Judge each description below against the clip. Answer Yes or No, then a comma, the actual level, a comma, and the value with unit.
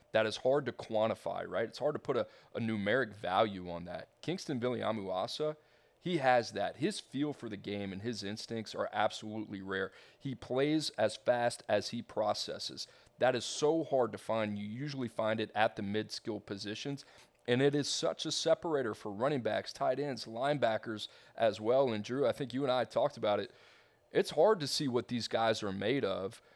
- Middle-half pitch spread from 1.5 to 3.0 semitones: No, average, 4.9 semitones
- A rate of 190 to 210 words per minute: Yes, average, 200 wpm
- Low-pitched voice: Yes, low, 115 Hz